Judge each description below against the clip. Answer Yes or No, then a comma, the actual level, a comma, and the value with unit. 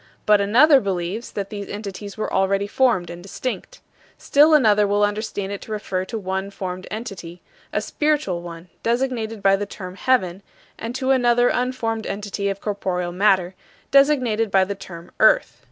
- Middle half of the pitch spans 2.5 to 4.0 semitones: Yes, average, 3.7 semitones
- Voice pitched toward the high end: Yes, high, 205 Hz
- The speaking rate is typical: Yes, average, 165 wpm